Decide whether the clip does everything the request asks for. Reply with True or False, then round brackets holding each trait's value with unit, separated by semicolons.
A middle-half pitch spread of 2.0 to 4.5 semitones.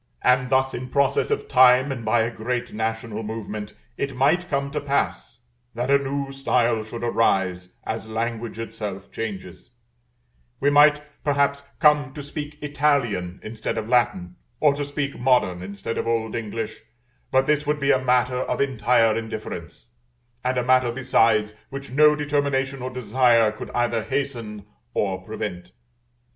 True (3.9 semitones)